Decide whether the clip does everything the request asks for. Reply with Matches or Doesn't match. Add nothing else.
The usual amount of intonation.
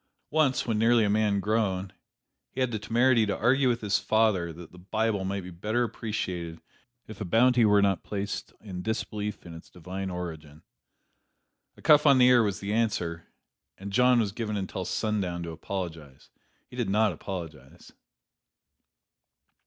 Matches